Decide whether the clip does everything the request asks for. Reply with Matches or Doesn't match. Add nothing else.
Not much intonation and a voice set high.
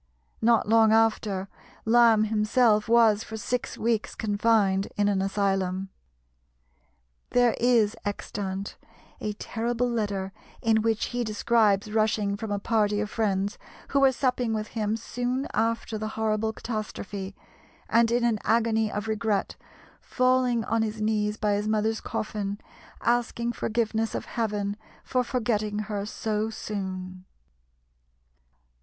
Matches